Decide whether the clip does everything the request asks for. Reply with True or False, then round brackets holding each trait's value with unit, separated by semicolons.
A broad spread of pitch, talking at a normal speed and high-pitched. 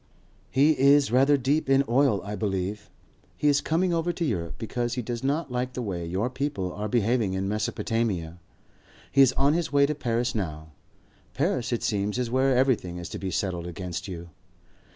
False (6.1 semitones; 190 wpm; 120 Hz)